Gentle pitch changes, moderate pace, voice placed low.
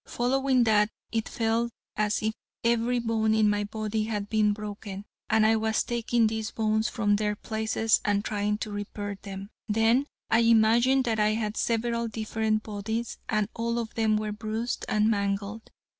No: narrow, 1.4 semitones; average, 170 wpm; high, 220 Hz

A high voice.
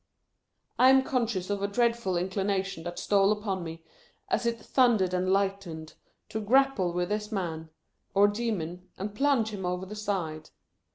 Yes: high, 200 Hz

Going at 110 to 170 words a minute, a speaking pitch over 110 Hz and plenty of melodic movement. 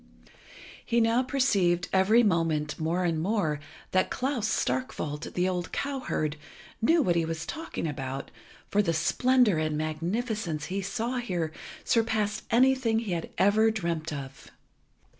Yes: average, 140 wpm; medium, 185 Hz; wide, 6.1 semitones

